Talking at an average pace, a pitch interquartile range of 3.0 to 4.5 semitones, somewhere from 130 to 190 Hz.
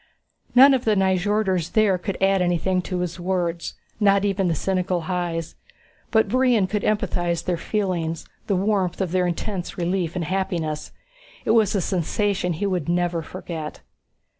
No: average, 160 wpm; narrow, 2.5 semitones; medium, 185 Hz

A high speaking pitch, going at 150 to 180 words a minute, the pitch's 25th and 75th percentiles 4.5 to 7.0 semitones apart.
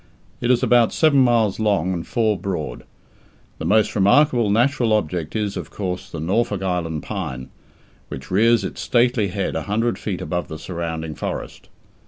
No: low, 100 Hz; average, 165 wpm; average, 4.8 semitones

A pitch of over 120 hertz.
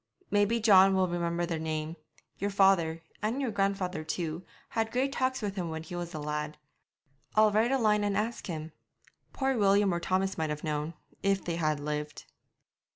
Yes: medium, 185 Hz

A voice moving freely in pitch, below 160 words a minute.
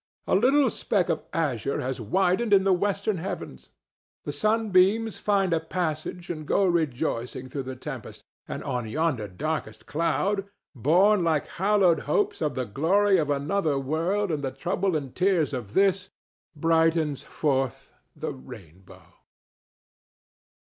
Yes: wide, 5.9 semitones; average, 140 wpm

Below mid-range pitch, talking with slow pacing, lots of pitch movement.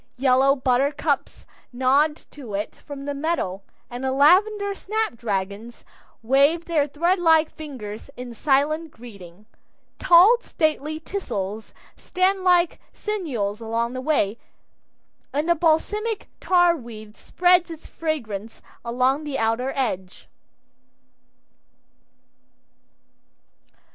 No: very high, 280 Hz; slow, 100 wpm; wide, 6.1 semitones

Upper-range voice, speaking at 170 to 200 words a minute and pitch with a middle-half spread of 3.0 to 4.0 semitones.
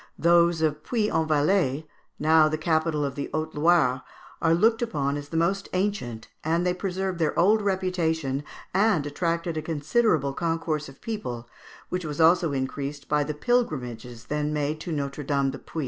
No: medium, 160 Hz; average, 175 wpm; average, 3.4 semitones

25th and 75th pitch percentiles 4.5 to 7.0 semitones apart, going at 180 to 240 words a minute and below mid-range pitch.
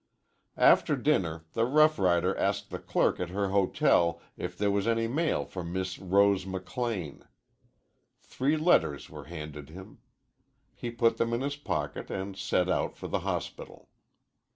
No: average, 4.8 semitones; average, 155 wpm; very low, 95 Hz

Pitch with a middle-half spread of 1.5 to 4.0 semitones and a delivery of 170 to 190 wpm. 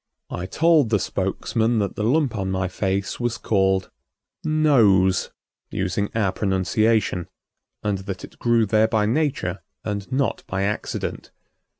No: average, 3.3 semitones; slow, 135 wpm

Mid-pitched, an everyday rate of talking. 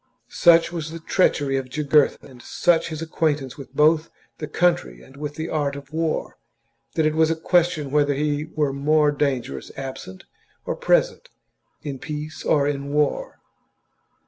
Yes: medium, 150 Hz; average, 160 wpm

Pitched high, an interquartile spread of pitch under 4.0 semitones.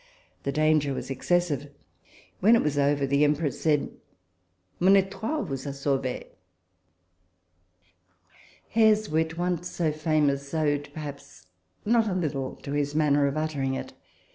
No: medium, 150 Hz; average, 3.4 semitones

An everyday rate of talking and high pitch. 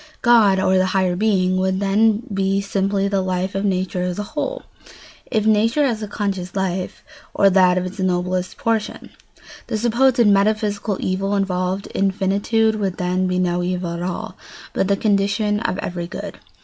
Yes: average, 175 wpm; high, 195 Hz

